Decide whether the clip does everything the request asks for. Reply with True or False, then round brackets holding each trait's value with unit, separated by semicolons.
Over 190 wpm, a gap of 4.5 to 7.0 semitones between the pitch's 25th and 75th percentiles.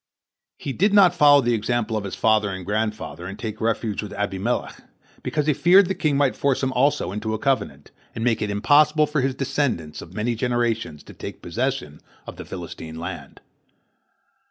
False (185 wpm; 5.5 semitones)